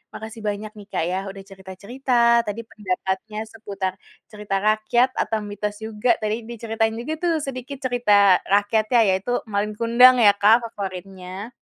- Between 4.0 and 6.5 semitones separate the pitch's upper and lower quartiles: No, average, 2.7 semitones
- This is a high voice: Yes, high, 215 Hz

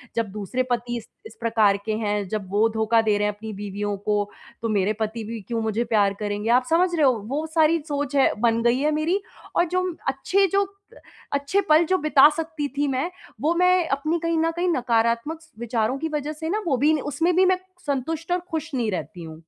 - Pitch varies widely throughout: Yes, wide, 6.7 semitones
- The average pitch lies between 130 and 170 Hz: No, very high, 255 Hz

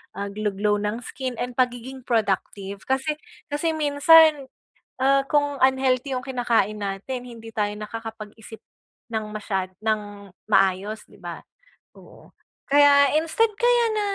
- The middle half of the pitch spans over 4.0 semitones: Yes, average, 5.1 semitones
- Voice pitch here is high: Yes, high, 245 Hz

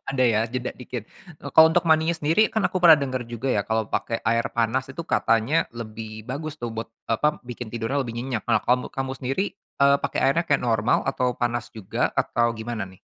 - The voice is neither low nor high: No, low, 125 Hz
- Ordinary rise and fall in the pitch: Yes, average, 3.6 semitones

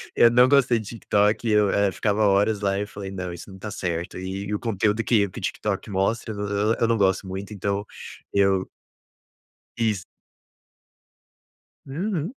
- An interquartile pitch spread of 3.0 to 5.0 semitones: No, narrow, 2.4 semitones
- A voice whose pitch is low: Yes, low, 100 Hz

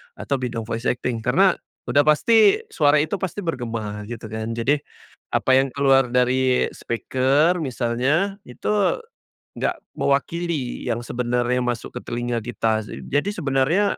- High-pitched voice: No, low, 130 Hz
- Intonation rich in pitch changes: No, average, 3.8 semitones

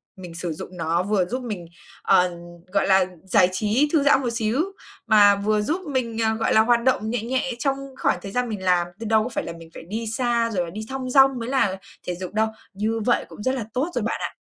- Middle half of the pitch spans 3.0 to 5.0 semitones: Yes, average, 4.7 semitones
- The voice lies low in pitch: No, high, 220 Hz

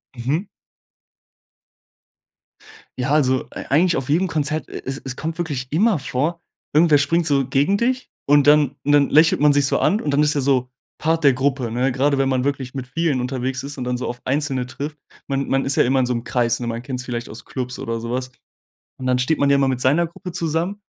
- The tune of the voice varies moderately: Yes, average, 3.1 semitones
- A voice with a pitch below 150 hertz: Yes, medium, 140 Hz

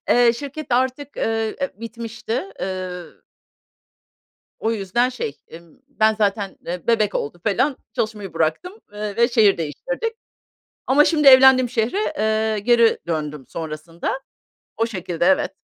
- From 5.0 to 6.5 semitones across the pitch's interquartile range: Yes, average, 5.3 semitones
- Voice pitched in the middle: No, high, 220 Hz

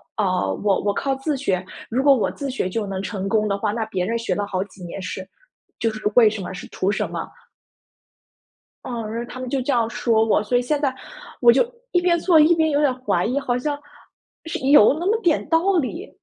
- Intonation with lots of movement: Yes, wide, 5.9 semitones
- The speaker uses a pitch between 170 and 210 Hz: No, high, 235 Hz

